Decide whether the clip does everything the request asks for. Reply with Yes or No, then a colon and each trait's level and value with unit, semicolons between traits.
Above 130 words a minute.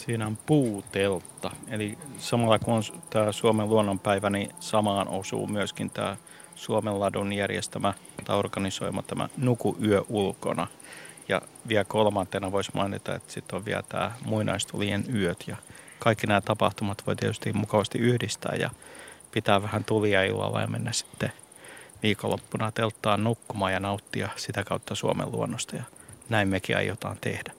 Yes: average, 140 wpm